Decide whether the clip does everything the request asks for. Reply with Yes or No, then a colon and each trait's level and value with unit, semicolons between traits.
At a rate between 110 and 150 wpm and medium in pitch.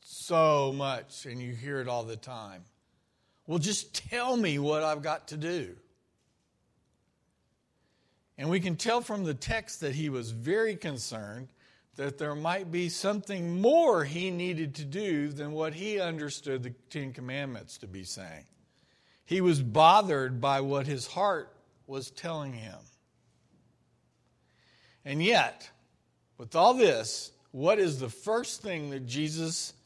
Yes: average, 145 wpm; medium, 150 Hz